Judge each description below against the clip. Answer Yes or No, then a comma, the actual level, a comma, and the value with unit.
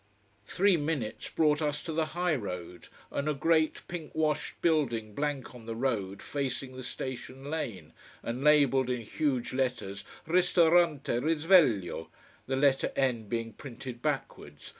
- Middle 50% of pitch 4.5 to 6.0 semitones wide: Yes, average, 4.9 semitones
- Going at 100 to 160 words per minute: Yes, average, 140 wpm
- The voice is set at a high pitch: No, low, 135 Hz